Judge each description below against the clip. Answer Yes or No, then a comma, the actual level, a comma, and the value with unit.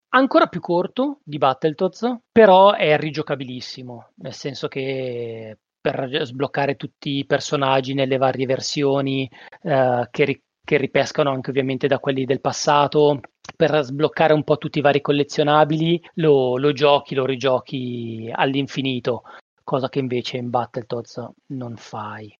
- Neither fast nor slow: Yes, average, 135 wpm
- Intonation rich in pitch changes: No, average, 2.7 semitones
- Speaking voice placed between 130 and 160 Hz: Yes, medium, 140 Hz